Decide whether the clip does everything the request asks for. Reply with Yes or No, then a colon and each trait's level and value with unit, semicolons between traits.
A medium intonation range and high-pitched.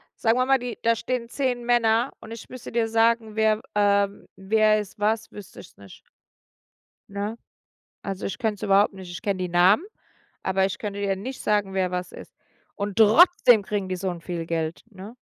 Yes: average, 3.0 semitones; high, 210 Hz